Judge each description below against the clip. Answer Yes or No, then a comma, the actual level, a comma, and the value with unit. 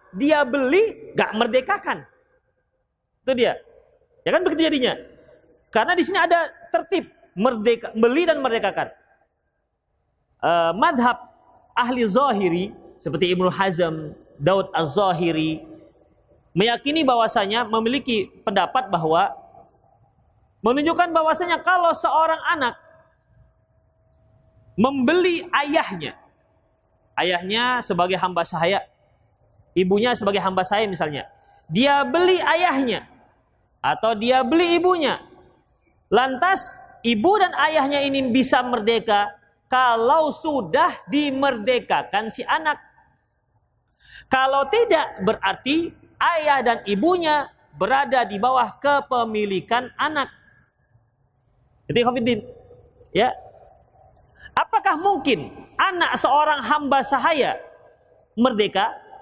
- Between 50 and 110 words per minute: Yes, average, 90 wpm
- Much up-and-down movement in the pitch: Yes, wide, 8.8 semitones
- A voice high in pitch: Yes, very high, 250 Hz